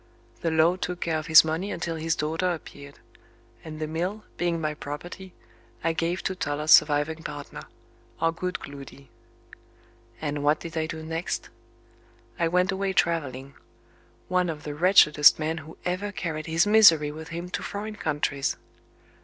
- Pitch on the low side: No, medium, 160 Hz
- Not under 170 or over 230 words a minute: No, average, 160 wpm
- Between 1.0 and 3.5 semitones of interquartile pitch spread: Yes, average, 2.8 semitones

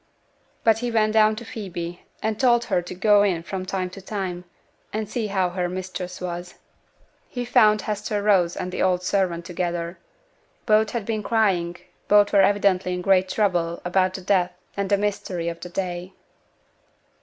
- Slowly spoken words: No, average, 175 wpm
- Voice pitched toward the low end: No, high, 190 Hz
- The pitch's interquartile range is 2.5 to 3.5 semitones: Yes, average, 2.9 semitones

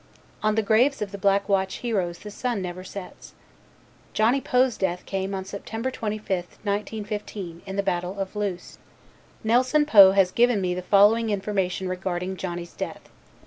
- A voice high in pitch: Yes, high, 200 Hz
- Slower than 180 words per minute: Yes, average, 160 wpm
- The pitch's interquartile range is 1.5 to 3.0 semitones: Yes, average, 2.7 semitones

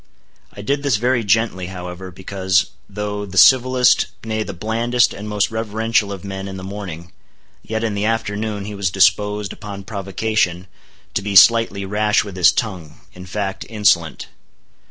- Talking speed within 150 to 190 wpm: Yes, average, 160 wpm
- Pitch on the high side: No, low, 105 Hz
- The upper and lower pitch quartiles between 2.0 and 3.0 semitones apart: Yes, narrow, 2.6 semitones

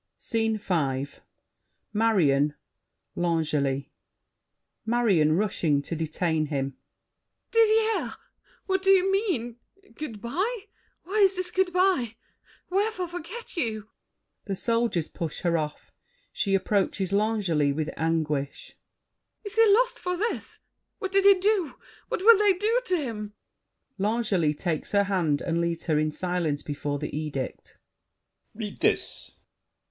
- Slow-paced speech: Yes, slow, 125 wpm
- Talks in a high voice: Yes, high, 210 Hz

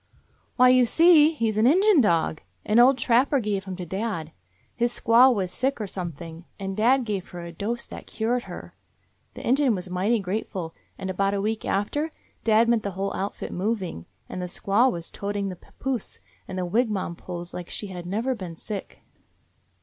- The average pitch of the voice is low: No, high, 205 Hz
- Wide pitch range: No, average, 4.7 semitones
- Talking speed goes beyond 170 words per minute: Yes, average, 190 wpm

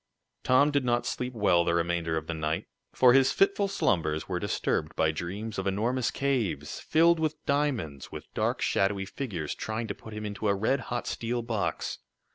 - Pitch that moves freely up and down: Yes, wide, 6.9 semitones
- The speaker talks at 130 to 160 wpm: No, average, 185 wpm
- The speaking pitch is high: No, low, 105 Hz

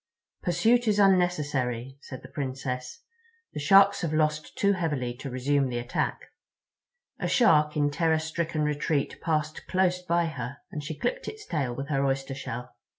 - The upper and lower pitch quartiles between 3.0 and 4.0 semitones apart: No, average, 4.4 semitones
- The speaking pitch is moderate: Yes, medium, 150 Hz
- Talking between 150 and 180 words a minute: Yes, average, 160 wpm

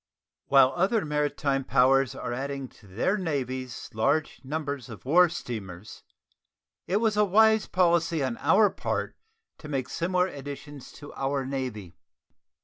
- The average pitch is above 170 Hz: No, medium, 140 Hz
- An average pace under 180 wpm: Yes, average, 140 wpm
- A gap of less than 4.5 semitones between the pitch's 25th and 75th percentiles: No, average, 4.9 semitones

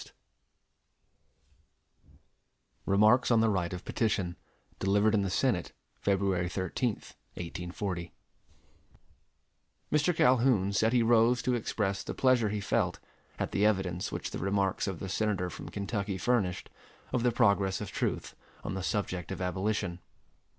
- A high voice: No, low, 100 Hz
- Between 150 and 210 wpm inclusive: No, slow, 135 wpm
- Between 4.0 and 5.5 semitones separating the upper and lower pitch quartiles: No, average, 3.2 semitones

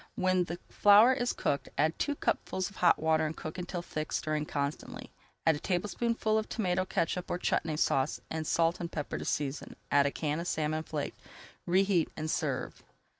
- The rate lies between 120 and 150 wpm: No, average, 185 wpm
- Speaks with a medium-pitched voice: Yes, medium, 165 Hz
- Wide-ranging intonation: No, average, 3.3 semitones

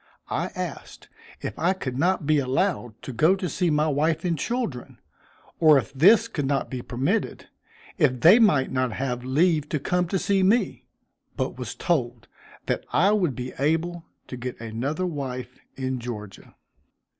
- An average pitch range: No, wide, 5.7 semitones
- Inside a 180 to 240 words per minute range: No, average, 165 wpm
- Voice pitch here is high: No, medium, 150 Hz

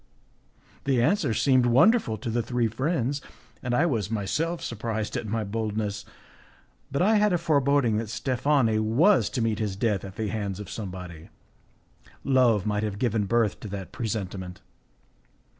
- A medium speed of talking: Yes, average, 160 wpm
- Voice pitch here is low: Yes, low, 115 Hz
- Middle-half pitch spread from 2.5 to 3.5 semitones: No, average, 4.2 semitones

